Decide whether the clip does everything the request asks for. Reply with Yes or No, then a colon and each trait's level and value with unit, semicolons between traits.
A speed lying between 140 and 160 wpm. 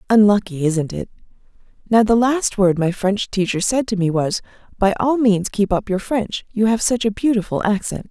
No: average, 200 wpm